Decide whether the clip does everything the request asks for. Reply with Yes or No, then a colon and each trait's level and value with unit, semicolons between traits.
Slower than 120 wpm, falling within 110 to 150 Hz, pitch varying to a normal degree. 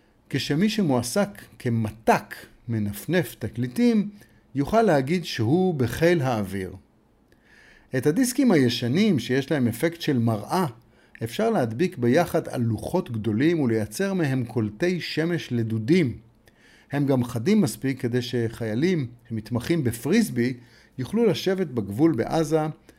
No: average, 105 wpm; low, 135 Hz; wide, 7.1 semitones